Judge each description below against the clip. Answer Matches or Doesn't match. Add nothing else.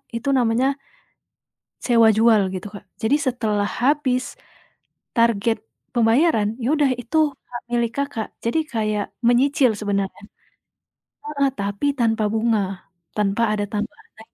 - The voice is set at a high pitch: Matches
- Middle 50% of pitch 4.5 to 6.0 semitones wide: Doesn't match